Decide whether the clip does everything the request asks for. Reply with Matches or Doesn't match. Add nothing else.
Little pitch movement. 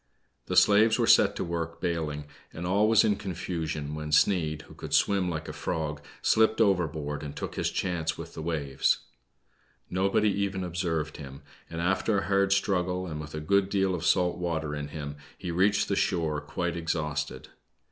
Doesn't match